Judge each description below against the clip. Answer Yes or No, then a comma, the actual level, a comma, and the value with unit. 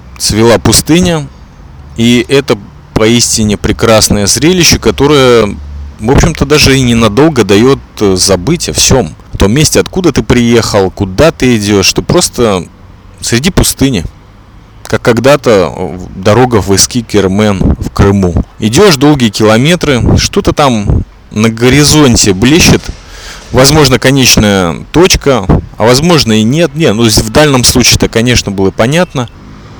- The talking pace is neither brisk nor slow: Yes, average, 125 wpm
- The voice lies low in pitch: Yes, low, 115 Hz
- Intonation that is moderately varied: Yes, average, 4.9 semitones